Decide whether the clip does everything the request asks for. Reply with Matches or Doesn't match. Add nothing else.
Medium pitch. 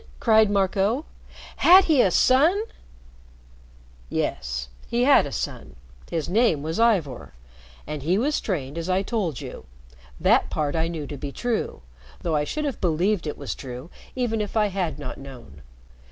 Matches